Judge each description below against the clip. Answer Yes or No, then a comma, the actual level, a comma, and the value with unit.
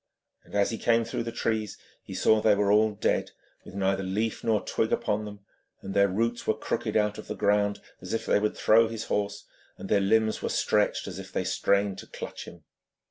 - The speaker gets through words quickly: Yes, fast, 210 wpm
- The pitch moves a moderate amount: No, narrow, 1.7 semitones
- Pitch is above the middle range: No, low, 105 Hz